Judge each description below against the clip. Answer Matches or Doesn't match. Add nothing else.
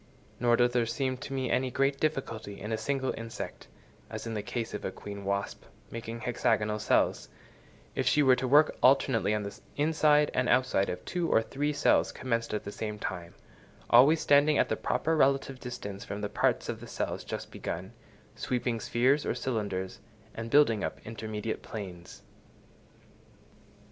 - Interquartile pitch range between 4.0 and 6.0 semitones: Matches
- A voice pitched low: Matches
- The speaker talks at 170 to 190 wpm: Matches